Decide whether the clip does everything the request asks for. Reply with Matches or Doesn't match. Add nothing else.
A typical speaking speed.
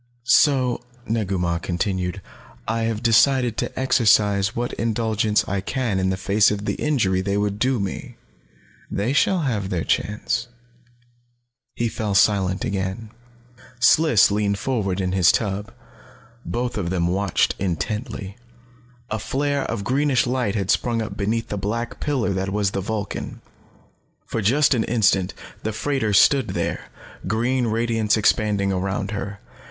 Matches